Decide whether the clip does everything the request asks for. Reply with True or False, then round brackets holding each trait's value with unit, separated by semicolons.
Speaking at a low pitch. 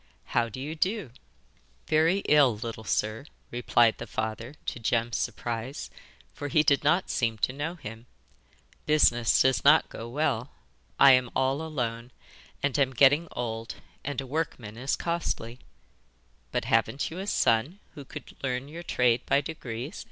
True (130 Hz)